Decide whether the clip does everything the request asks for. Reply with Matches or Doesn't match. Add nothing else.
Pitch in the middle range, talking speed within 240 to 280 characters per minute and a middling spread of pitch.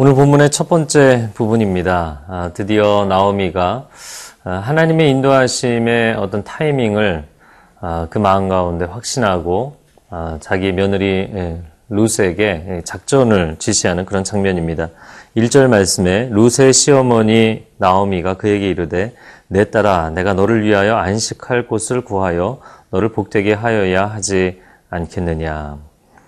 Doesn't match